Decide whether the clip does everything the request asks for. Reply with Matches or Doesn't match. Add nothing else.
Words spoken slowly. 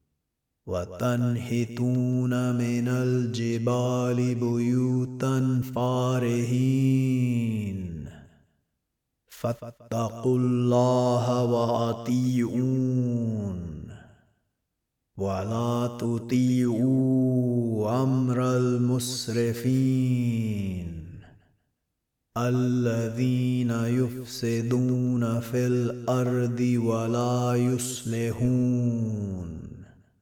Matches